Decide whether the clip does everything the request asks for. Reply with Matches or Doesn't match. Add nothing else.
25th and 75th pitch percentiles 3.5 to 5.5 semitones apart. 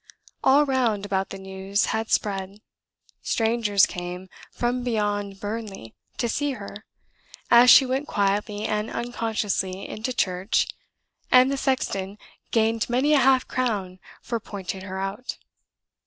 Matches